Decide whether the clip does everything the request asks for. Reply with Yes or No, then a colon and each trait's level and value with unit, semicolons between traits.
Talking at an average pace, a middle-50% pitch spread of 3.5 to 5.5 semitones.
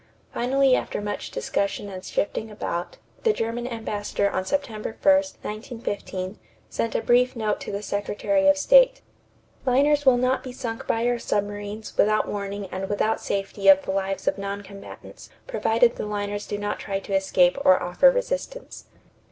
Yes: average, 165 wpm; average, 4.1 semitones